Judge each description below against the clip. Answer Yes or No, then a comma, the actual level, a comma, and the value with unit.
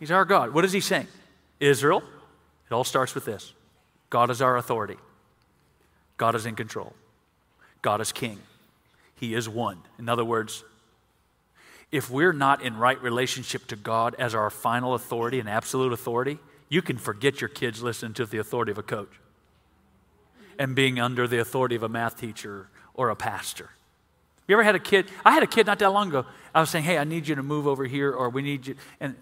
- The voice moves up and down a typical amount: Yes, average, 4.0 semitones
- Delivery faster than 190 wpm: Yes, average, 200 wpm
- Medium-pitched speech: No, low, 125 Hz